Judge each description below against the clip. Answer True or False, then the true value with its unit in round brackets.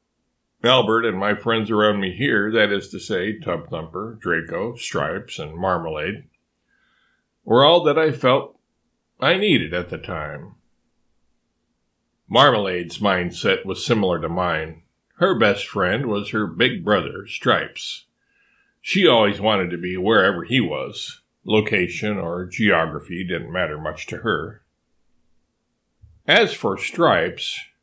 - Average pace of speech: False (125 wpm)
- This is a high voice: False (95 Hz)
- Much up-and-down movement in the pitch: False (3.4 semitones)